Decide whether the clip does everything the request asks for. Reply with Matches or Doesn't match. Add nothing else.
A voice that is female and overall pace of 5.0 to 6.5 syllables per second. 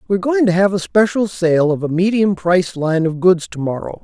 Doesn't match